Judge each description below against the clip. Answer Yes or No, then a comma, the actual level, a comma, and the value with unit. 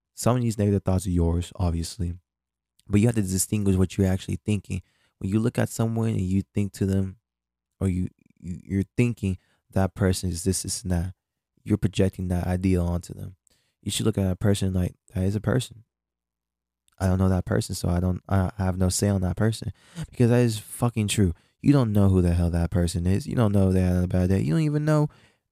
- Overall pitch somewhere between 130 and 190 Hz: No, very low, 95 Hz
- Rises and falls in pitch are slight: No, average, 3.2 semitones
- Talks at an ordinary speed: No, fast, 225 wpm